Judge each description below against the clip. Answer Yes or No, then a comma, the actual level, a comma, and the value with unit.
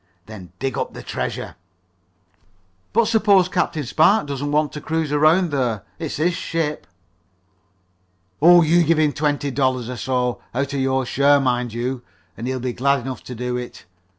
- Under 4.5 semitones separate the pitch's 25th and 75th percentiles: Yes, average, 3.9 semitones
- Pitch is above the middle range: No, medium, 140 Hz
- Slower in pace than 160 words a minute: No, average, 175 wpm